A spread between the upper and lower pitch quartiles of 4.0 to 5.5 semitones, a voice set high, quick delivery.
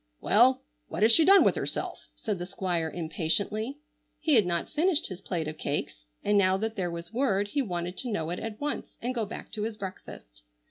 Yes: average, 5.1 semitones; high, 205 Hz; fast, 215 wpm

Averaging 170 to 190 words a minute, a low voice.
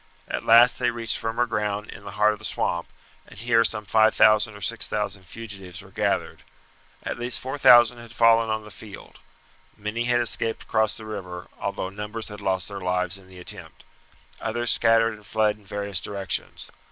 Yes: average, 180 wpm; low, 105 Hz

